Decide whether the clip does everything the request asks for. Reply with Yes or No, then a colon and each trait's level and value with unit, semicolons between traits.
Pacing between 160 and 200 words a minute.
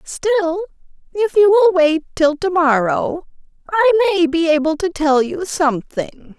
No: average, 150 wpm